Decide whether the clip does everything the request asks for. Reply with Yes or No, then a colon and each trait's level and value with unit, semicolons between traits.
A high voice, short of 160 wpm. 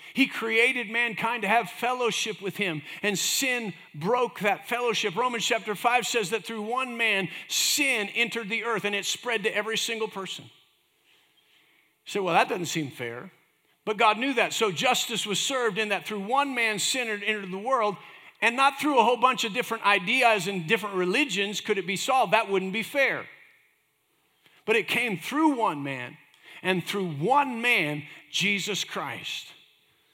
No: high, 220 Hz; average, 175 wpm